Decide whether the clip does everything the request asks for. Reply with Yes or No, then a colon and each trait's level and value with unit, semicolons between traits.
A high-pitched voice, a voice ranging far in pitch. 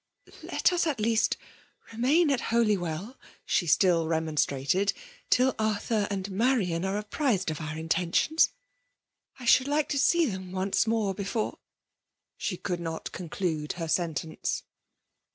Yes: high, 195 Hz; wide, 5.9 semitones